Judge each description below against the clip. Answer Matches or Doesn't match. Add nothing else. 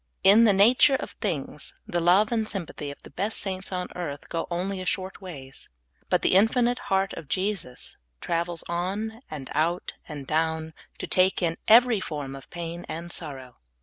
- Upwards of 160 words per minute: Matches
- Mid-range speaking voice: Matches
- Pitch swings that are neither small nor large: Matches